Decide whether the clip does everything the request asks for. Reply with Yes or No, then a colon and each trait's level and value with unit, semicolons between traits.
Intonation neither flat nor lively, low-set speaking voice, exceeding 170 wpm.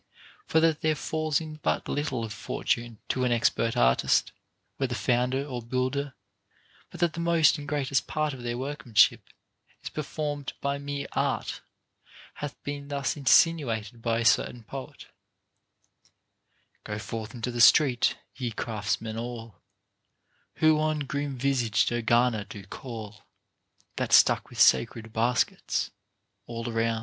No: average, 3.9 semitones; low, 125 Hz; average, 140 wpm